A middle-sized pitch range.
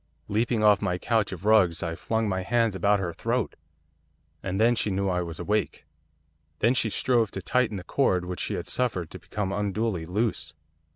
Yes: average, 3.7 semitones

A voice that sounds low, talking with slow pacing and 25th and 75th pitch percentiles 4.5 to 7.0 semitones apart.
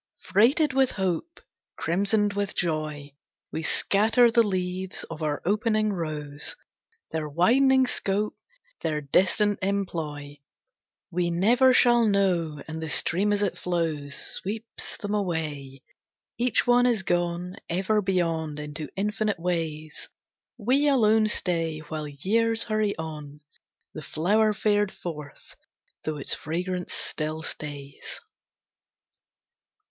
No: medium, 180 Hz; slow, 115 wpm; wide, 5.4 semitones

